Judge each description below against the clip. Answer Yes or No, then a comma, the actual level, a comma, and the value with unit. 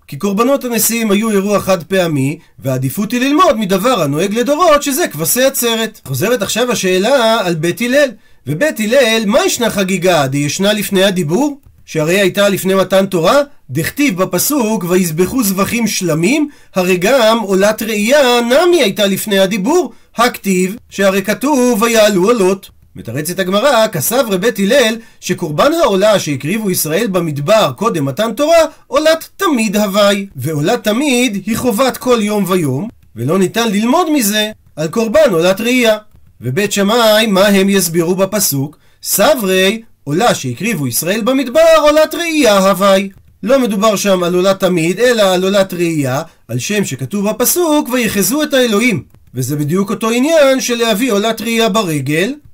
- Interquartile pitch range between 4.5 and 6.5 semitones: Yes, average, 4.9 semitones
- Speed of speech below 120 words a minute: No, average, 145 wpm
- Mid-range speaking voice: No, high, 205 Hz